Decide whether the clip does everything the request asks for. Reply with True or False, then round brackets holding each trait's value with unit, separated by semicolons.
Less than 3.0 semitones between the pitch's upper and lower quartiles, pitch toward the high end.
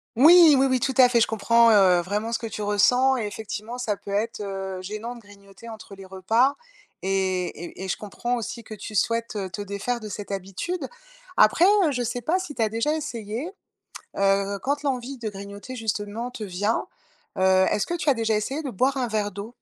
False (3.7 semitones; 220 Hz)